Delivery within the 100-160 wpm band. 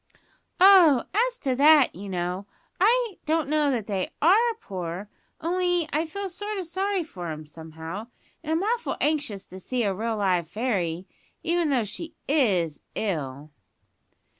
Yes: average, 155 wpm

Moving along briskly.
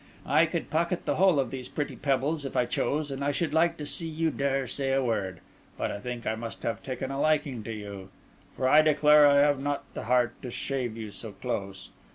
Yes: fast, 235 wpm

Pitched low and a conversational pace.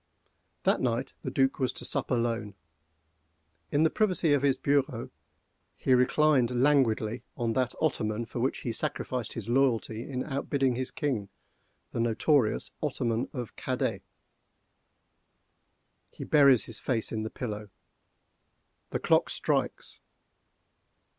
No: low, 125 Hz; slow, 125 wpm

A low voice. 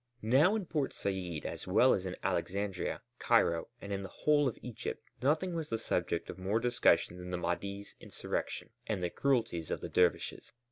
Yes: low, 100 Hz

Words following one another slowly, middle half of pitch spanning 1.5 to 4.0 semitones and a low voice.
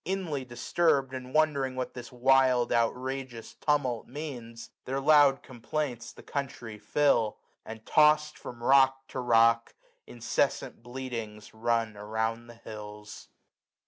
Yes: slow, 125 wpm; average, 3.0 semitones; low, 125 Hz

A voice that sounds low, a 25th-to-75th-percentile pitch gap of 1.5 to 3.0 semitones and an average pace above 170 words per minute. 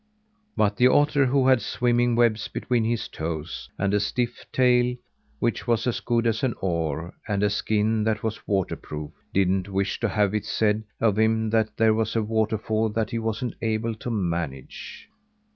Yes: low, 110 Hz; narrow, 2.6 semitones; average, 180 wpm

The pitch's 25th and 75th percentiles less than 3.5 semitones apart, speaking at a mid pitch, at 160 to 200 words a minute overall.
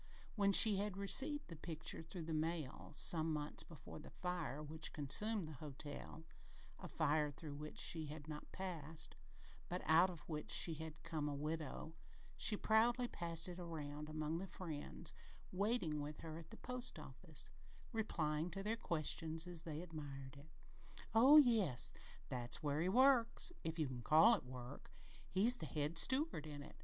No: average, 4.1 semitones; medium, 160 Hz; average, 170 wpm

